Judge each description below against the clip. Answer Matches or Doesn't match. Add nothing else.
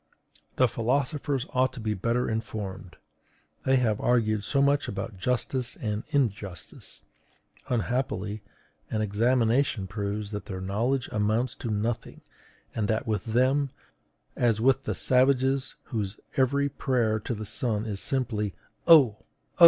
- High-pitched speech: Doesn't match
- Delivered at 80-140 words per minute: Matches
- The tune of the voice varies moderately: Matches